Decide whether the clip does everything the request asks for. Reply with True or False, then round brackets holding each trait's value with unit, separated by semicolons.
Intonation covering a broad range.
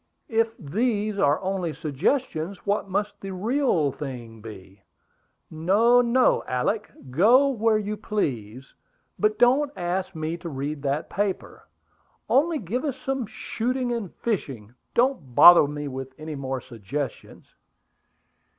True (8.2 semitones)